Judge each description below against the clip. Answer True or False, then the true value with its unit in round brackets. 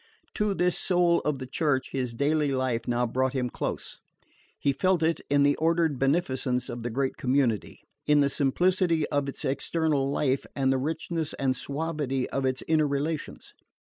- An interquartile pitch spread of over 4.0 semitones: False (3.5 semitones)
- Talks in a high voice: False (140 Hz)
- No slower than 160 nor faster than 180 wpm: True (175 wpm)